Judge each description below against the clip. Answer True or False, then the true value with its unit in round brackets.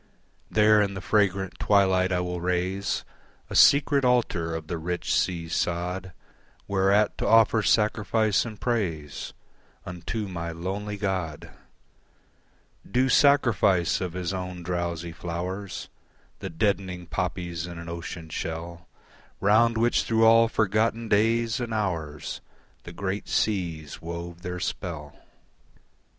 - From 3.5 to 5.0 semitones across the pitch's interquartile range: True (3.8 semitones)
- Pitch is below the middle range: True (95 Hz)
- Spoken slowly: True (125 wpm)